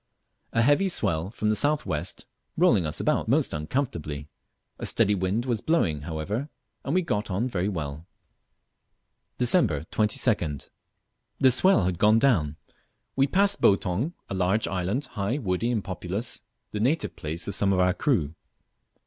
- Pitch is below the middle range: Yes, low, 105 Hz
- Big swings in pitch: Yes, wide, 6.4 semitones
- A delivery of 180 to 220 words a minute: No, average, 155 wpm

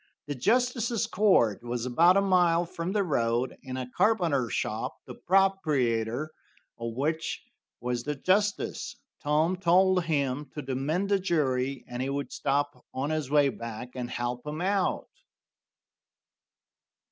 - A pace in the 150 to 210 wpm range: No, average, 140 wpm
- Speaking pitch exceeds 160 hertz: No, medium, 150 Hz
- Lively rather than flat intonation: Yes, wide, 6.3 semitones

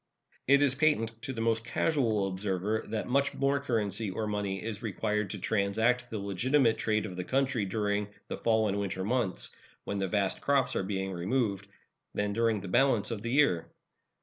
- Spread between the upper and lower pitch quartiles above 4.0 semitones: No, average, 3.7 semitones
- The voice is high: No, low, 110 Hz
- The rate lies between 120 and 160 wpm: No, average, 185 wpm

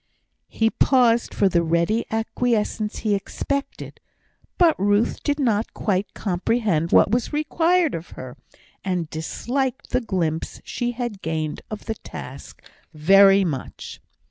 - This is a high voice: Yes, high, 210 Hz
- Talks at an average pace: No, slow, 130 wpm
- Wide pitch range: Yes, wide, 5.7 semitones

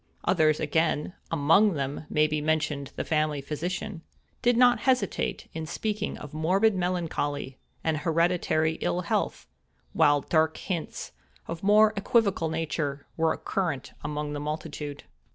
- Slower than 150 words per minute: Yes, slow, 135 wpm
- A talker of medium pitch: Yes, medium, 160 Hz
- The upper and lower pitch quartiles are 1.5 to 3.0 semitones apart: No, average, 3.6 semitones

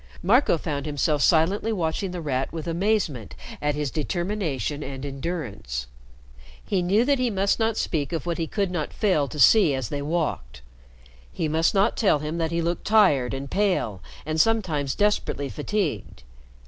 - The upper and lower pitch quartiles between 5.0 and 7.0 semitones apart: Yes, wide, 5.5 semitones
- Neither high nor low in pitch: Yes, medium, 160 Hz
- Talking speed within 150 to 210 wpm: Yes, average, 170 wpm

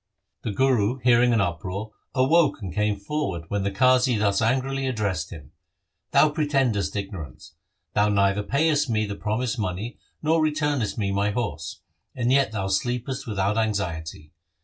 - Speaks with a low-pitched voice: Yes, low, 110 Hz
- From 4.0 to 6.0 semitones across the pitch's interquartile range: Yes, average, 4.7 semitones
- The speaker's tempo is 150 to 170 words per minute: Yes, average, 155 wpm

